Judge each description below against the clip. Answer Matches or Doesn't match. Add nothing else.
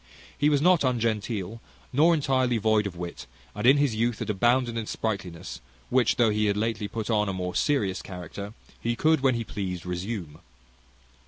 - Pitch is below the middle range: Matches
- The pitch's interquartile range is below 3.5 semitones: Doesn't match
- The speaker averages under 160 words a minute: Doesn't match